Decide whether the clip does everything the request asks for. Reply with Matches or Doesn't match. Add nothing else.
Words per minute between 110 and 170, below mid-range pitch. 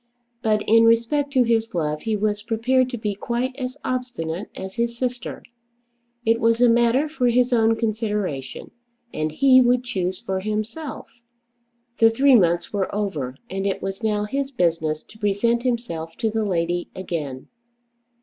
Doesn't match